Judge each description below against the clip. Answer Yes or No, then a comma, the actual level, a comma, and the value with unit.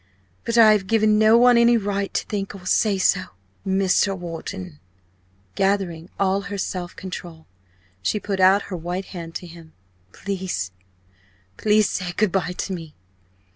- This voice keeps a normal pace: Yes, average, 165 wpm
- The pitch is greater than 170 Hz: Yes, high, 190 Hz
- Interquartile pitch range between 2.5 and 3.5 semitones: Yes, average, 2.9 semitones